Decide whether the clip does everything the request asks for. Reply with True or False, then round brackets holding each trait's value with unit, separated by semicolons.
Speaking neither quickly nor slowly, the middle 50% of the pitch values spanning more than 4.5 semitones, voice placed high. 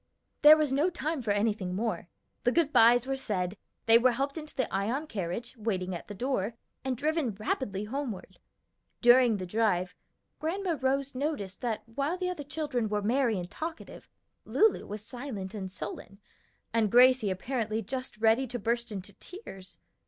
True (165 wpm; 5.1 semitones; 235 Hz)